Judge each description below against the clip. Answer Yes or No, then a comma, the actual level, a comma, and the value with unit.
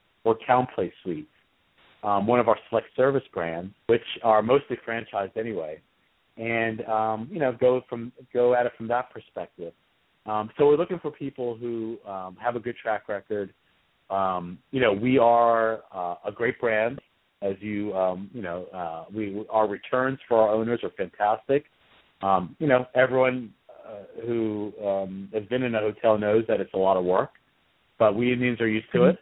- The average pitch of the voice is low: Yes, low, 115 Hz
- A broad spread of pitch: No, average, 3.2 semitones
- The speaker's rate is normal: Yes, average, 185 wpm